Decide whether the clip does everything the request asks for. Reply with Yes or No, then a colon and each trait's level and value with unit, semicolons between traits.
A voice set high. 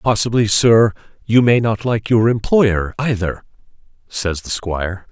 No: low, 110 Hz